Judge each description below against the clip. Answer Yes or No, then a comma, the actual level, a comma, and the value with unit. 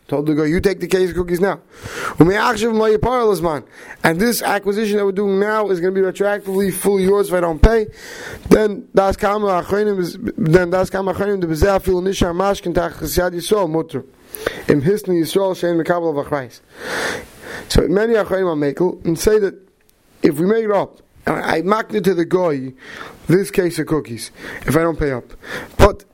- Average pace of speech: No, slow, 125 wpm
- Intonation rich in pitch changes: No, average, 3.3 semitones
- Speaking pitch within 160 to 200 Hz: Yes, high, 190 Hz